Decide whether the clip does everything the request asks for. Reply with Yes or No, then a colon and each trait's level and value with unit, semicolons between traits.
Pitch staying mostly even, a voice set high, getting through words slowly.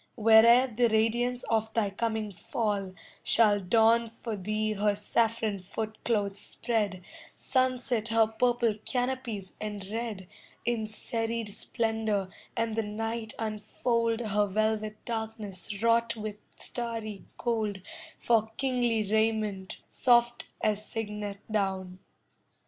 Yes: narrow, 1.9 semitones; high, 220 Hz; slow, 110 wpm